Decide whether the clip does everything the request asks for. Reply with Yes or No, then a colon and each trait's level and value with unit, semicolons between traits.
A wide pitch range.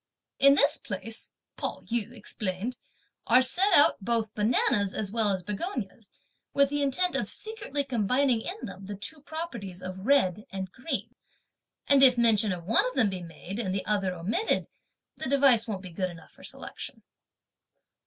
Yes: wide, 6.1 semitones